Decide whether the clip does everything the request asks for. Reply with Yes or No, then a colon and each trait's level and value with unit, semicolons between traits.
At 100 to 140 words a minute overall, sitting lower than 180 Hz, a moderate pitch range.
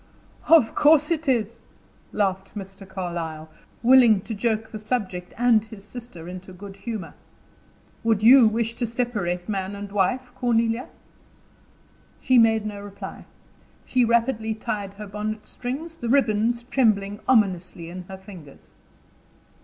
No: slow, 135 wpm; high, 215 Hz; average, 3.6 semitones